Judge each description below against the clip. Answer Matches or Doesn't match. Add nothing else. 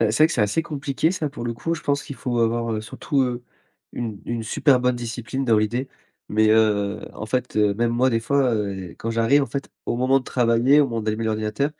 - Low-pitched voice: Matches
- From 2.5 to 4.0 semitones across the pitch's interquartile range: Matches